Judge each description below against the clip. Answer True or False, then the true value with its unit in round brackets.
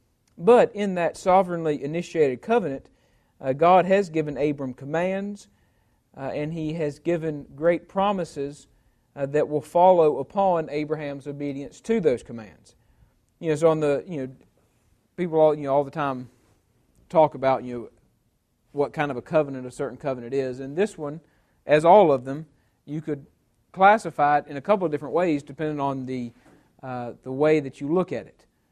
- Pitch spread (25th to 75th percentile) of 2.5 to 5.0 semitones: True (3.8 semitones)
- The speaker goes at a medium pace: True (175 wpm)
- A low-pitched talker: False (145 Hz)